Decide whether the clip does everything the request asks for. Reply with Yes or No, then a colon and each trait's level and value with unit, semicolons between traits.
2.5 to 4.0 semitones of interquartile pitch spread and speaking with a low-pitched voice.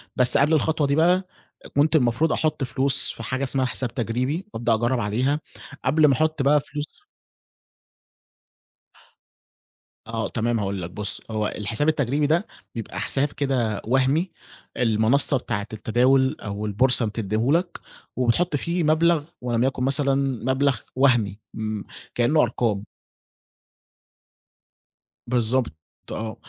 No: average, 4.5 semitones; low, 130 Hz